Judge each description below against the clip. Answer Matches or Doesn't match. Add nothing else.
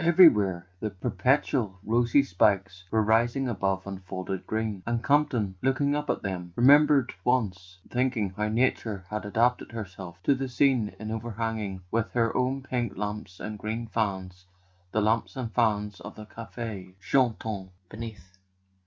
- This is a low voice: Matches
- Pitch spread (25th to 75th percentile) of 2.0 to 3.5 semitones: Doesn't match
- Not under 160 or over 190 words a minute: Doesn't match